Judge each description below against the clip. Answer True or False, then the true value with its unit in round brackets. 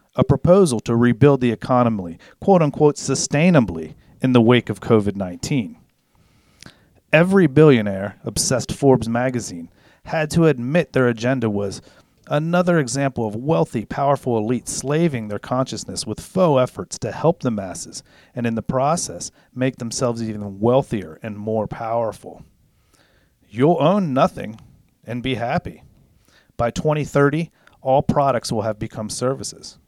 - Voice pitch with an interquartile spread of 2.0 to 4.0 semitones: False (4.6 semitones)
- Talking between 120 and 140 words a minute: True (135 wpm)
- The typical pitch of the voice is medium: False (125 Hz)